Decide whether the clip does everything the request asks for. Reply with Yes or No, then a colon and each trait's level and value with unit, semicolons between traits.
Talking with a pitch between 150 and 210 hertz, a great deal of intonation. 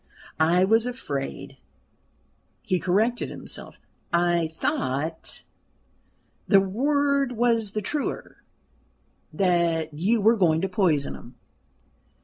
Yes: medium, 185 Hz; wide, 5.8 semitones